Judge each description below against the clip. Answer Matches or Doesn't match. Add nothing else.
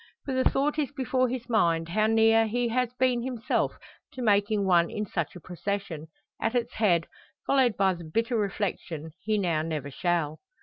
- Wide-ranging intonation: Matches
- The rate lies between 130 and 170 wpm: Doesn't match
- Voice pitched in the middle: Doesn't match